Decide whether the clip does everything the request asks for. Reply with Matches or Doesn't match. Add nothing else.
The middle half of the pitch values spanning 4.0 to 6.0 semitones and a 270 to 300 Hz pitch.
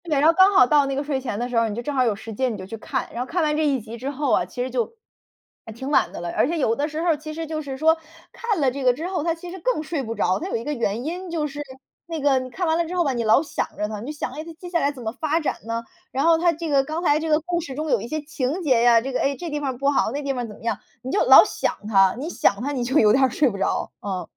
Matches